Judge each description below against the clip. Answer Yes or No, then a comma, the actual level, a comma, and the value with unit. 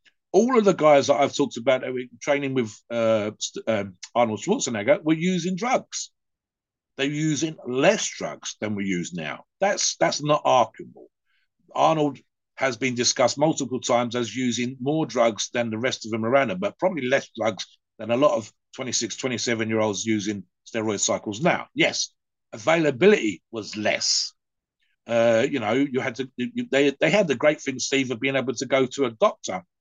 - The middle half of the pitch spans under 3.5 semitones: No, average, 3.9 semitones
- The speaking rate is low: No, average, 175 wpm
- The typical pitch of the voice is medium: No, low, 130 Hz